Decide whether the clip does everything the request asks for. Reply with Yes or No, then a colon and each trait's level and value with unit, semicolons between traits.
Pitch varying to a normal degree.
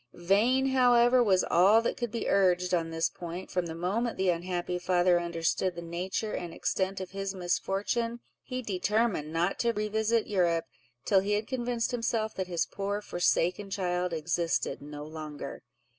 Yes: average, 4.0 semitones